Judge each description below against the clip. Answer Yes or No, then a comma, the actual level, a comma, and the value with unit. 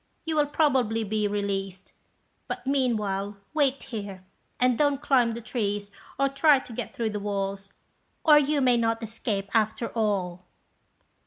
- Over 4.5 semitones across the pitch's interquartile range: Yes, average, 4.9 semitones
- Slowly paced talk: No, average, 150 wpm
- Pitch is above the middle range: Yes, high, 225 Hz